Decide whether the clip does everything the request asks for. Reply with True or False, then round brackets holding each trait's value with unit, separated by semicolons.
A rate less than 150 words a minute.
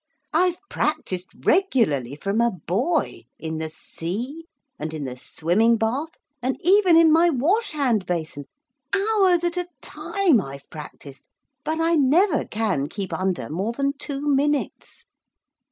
True (140 wpm)